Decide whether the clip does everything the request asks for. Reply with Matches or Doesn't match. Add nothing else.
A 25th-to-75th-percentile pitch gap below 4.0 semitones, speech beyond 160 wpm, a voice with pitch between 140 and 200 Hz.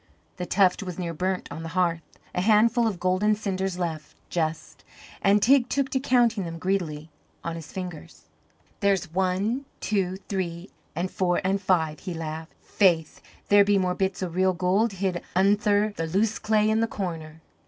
Matches